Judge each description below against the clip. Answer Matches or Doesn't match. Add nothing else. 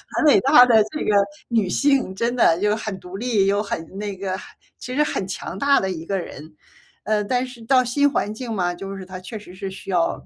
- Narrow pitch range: Doesn't match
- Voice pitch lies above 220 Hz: Doesn't match